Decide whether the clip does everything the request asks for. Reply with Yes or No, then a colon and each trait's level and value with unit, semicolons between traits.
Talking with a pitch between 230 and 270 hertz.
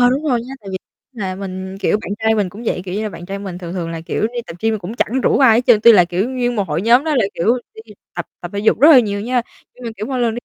No: high, 220 Hz